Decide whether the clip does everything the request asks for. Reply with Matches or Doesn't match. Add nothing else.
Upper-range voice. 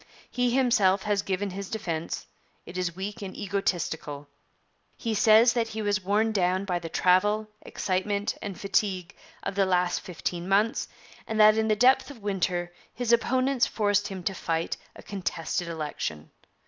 Matches